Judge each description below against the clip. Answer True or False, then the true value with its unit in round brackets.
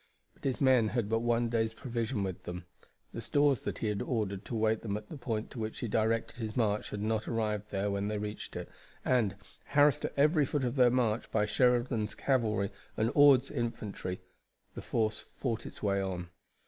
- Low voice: True (110 Hz)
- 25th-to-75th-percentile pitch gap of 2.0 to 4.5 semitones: True (2.9 semitones)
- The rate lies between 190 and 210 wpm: True (200 wpm)